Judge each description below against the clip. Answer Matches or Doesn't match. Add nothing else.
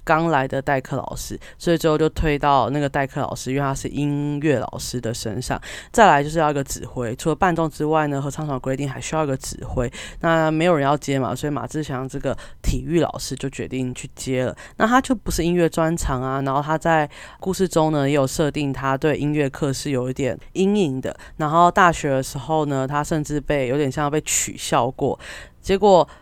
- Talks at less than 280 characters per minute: Doesn't match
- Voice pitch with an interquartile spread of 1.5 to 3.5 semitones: Matches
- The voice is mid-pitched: Matches